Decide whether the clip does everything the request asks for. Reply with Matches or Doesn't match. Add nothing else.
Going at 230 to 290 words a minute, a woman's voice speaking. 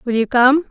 Matches